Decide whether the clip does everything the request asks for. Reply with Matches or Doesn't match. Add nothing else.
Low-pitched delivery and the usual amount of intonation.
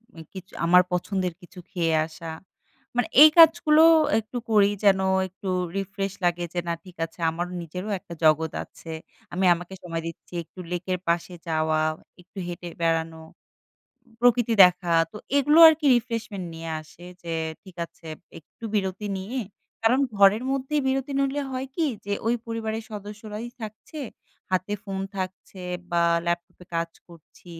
Doesn't match